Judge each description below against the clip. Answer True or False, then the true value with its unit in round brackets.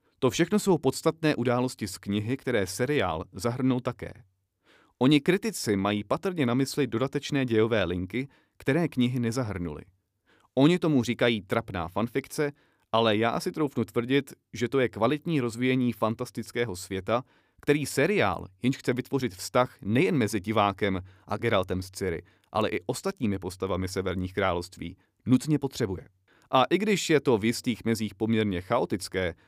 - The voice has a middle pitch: False (120 Hz)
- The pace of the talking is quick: False (145 wpm)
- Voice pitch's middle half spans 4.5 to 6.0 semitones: True (4.9 semitones)